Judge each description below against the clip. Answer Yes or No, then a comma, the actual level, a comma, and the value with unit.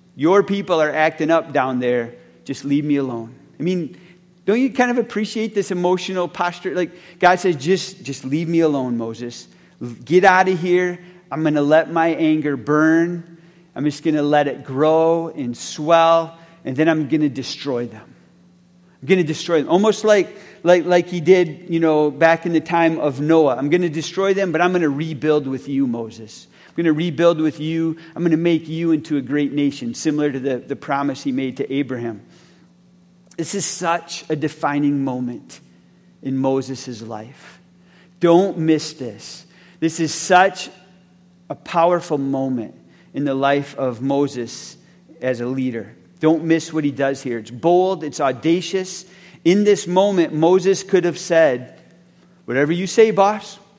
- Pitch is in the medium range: Yes, medium, 165 Hz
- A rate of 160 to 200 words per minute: Yes, average, 180 wpm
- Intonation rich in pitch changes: No, average, 4.0 semitones